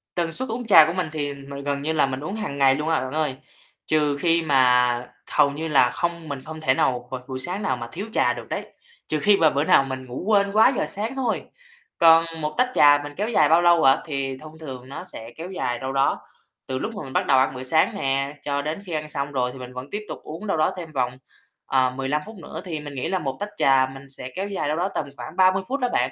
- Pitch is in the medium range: Yes, medium, 150 Hz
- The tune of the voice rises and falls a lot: No, average, 4.3 semitones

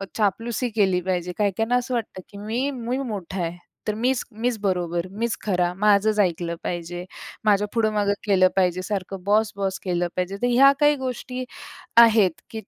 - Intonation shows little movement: No, average, 3.8 semitones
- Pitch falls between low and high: No, high, 205 Hz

